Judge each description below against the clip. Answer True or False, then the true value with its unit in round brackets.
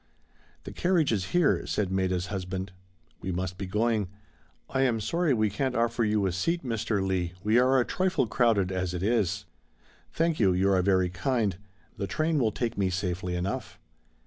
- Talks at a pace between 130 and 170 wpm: False (180 wpm)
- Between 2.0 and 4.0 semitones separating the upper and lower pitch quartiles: False (4.7 semitones)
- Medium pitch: False (105 Hz)